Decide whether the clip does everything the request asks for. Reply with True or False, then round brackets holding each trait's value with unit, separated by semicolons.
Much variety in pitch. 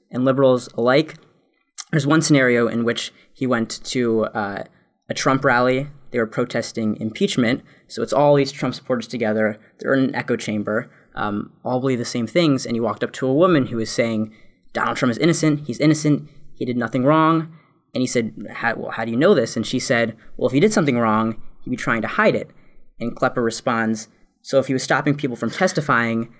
False (3.7 semitones)